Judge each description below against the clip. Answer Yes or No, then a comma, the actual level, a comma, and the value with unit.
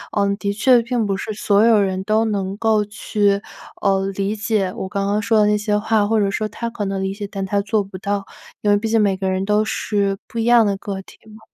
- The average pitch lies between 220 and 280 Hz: No, high, 205 Hz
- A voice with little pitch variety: Yes, narrow, 1.6 semitones